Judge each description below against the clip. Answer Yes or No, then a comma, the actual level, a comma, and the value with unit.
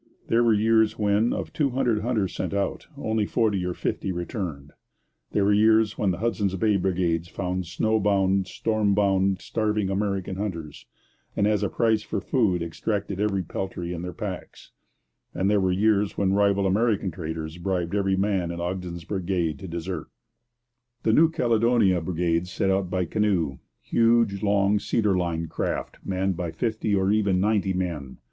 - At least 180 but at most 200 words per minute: No, average, 165 wpm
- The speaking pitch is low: Yes, very low, 95 Hz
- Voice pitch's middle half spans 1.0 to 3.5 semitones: Yes, average, 2.9 semitones